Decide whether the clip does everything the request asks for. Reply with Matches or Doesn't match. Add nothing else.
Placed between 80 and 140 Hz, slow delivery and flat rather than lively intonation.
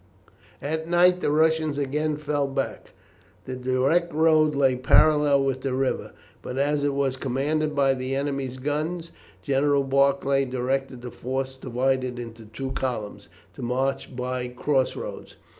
Doesn't match